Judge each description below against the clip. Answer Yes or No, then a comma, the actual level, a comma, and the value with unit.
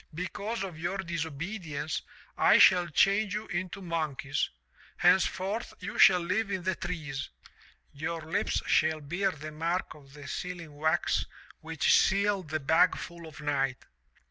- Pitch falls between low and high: Yes, medium, 170 Hz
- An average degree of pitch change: Yes, average, 3.5 semitones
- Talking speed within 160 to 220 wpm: No, average, 145 wpm